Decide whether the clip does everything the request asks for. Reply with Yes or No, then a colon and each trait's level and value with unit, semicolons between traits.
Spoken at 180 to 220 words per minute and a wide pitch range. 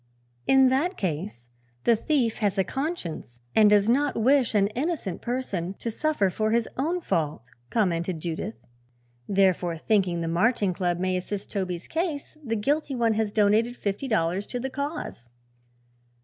No: average, 155 wpm; wide, 6.2 semitones